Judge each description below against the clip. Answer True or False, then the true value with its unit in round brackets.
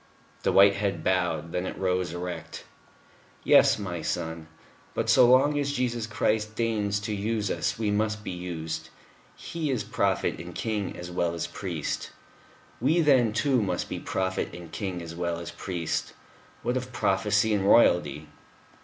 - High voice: False (100 Hz)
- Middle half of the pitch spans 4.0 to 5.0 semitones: True (4.3 semitones)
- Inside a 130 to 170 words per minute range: True (160 wpm)